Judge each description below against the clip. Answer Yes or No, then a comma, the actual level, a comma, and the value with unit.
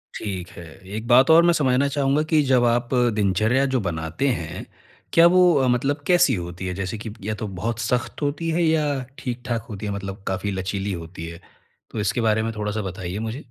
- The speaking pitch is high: No, low, 110 Hz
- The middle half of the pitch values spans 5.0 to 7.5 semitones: Yes, wide, 5.6 semitones